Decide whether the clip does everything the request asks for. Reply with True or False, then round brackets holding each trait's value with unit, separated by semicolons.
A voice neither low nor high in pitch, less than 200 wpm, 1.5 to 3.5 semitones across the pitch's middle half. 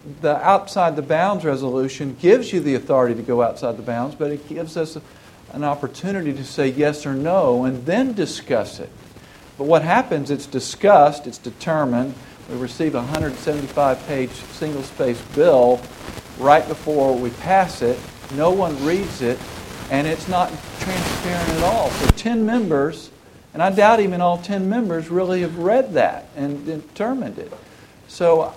False (150 Hz; 160 wpm; 5.1 semitones)